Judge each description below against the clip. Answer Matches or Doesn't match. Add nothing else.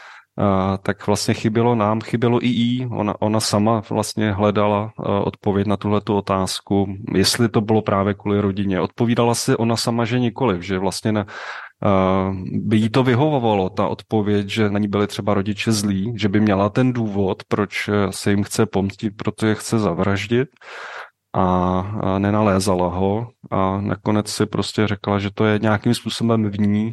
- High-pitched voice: Doesn't match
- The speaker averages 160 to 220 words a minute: Matches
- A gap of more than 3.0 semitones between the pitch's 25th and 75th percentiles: Doesn't match